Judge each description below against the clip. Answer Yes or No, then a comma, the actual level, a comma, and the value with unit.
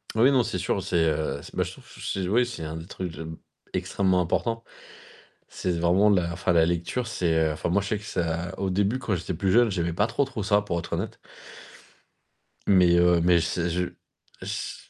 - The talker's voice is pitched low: Yes, very low, 90 Hz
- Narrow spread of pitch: No, average, 3.3 semitones